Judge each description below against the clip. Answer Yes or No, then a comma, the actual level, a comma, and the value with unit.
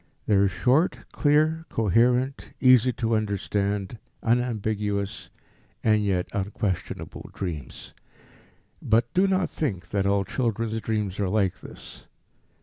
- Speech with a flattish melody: No, average, 3.7 semitones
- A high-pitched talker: No, low, 110 Hz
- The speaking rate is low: Yes, slow, 115 wpm